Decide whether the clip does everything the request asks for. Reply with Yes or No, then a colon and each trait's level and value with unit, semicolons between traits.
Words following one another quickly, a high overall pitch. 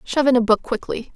Yes: fast, 260 wpm; high, 240 Hz